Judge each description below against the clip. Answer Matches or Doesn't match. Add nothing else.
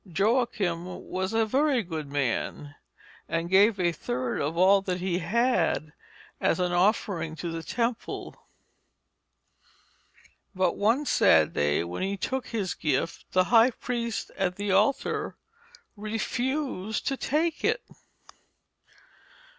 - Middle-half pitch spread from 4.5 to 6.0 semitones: Matches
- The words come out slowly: Matches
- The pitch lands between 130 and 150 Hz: Doesn't match